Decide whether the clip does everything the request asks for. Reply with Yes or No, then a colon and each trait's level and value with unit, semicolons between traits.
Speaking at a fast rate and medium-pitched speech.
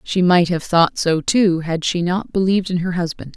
Yes: fast, 230 wpm; medium, 175 Hz